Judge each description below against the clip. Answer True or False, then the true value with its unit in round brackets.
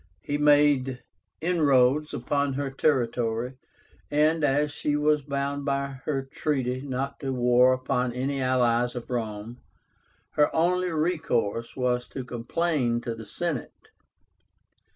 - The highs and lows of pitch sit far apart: False (3.1 semitones)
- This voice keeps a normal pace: False (125 wpm)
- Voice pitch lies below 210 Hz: True (135 Hz)